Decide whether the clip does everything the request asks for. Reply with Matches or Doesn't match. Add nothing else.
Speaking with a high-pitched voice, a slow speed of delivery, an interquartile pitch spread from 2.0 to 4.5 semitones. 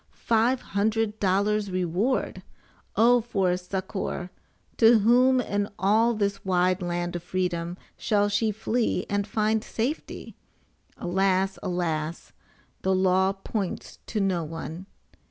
Matches